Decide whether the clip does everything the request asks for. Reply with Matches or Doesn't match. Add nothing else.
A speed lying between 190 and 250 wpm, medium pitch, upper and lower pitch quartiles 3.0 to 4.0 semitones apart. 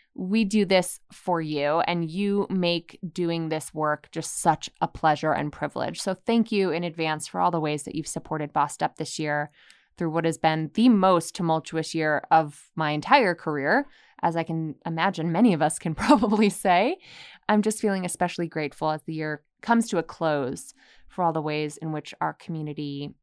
Matches